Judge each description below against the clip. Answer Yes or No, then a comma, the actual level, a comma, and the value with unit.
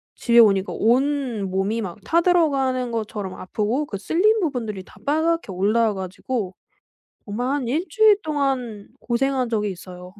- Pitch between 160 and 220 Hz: No, high, 235 Hz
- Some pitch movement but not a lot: No, wide, 5.9 semitones